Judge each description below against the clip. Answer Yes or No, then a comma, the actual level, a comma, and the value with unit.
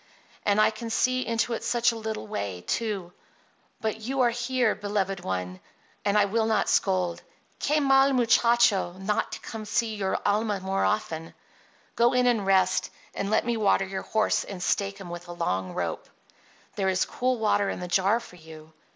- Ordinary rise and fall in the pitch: Yes, average, 3.9 semitones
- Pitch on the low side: No, high, 205 Hz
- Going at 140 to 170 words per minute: No, average, 190 wpm